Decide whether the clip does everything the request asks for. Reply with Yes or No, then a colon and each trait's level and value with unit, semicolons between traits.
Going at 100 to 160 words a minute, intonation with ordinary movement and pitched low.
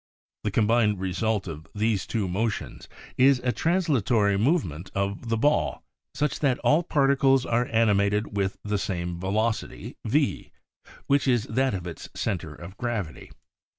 Yes: average, 145 wpm; average, 4.6 semitones; low, 110 Hz